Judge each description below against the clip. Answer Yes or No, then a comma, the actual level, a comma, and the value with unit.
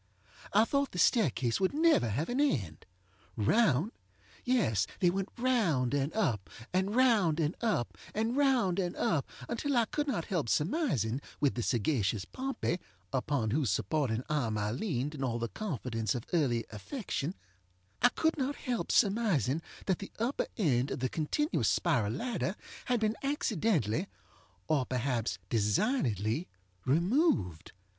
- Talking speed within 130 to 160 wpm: Yes, average, 145 wpm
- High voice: No, medium, 155 Hz